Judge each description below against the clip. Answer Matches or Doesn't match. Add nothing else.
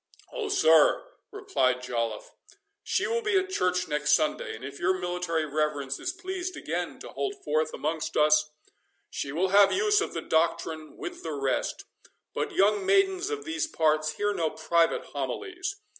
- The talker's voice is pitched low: Doesn't match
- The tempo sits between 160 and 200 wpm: Matches